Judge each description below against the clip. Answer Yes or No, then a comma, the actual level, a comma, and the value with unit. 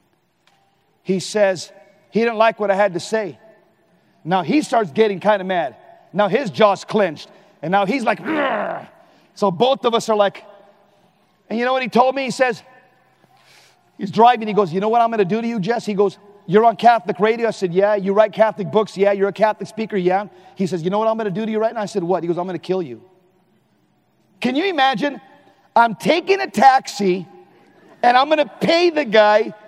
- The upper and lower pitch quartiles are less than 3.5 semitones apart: Yes, average, 2.8 semitones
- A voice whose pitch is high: Yes, high, 210 Hz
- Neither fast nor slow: No, fast, 215 wpm